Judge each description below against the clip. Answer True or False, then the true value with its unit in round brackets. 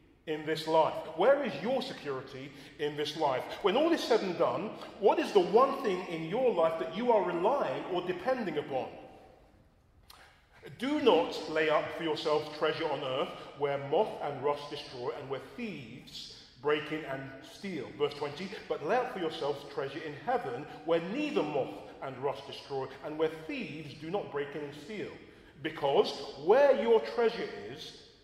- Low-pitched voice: False (160 Hz)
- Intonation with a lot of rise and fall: True (7.0 semitones)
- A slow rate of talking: False (175 wpm)